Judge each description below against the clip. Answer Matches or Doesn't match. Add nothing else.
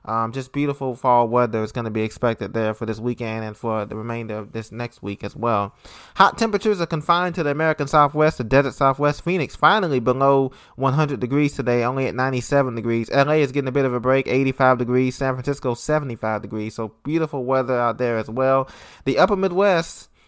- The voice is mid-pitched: Doesn't match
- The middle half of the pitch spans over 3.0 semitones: Matches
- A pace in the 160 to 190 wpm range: Doesn't match